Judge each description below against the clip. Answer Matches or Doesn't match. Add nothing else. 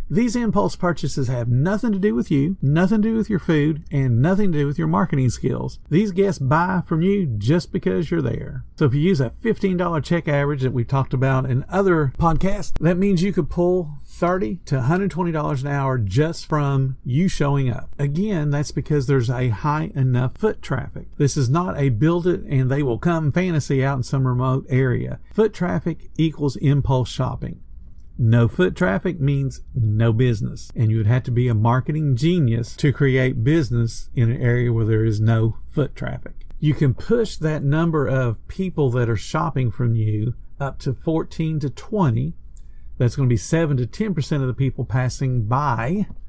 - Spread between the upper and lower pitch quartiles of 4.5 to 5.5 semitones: Matches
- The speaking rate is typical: Matches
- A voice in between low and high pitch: Matches